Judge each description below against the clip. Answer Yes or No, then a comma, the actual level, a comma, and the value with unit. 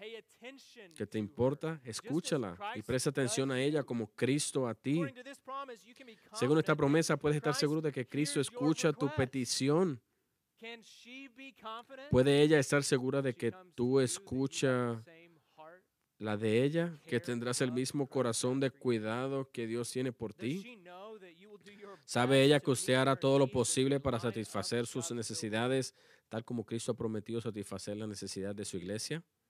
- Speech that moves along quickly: No, average, 145 wpm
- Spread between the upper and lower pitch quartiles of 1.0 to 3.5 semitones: No, average, 5.1 semitones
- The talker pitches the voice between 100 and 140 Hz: Yes, low, 135 Hz